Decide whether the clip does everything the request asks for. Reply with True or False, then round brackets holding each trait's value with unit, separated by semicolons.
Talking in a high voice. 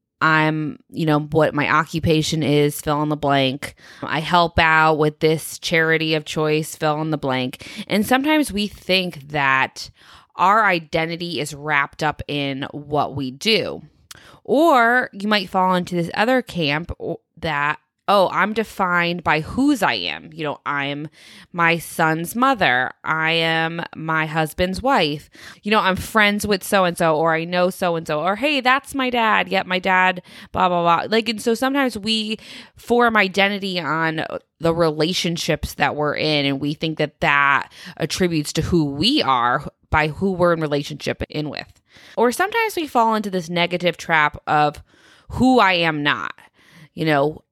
False (165 Hz)